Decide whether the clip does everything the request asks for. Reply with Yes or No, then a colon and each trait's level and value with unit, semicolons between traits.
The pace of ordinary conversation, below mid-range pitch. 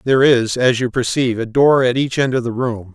No: fast, 225 wpm; low, 125 Hz